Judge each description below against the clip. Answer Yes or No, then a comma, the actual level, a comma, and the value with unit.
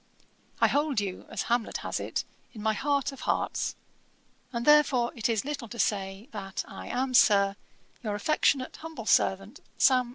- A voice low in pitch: No, high, 235 Hz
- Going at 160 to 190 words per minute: Yes, average, 165 wpm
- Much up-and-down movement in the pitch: No, average, 4.8 semitones